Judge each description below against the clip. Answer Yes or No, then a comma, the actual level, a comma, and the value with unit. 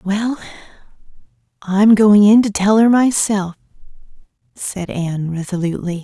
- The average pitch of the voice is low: No, high, 200 Hz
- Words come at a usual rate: No, slow, 110 wpm